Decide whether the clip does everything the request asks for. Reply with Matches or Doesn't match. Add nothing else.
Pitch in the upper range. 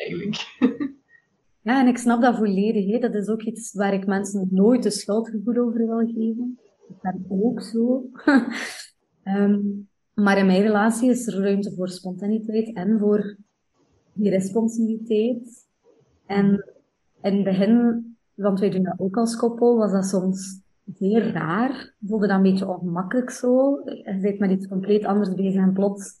Matches